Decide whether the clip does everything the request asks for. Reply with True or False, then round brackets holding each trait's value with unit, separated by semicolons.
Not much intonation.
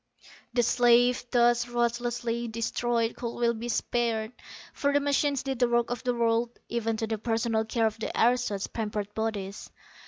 True (1.3 semitones)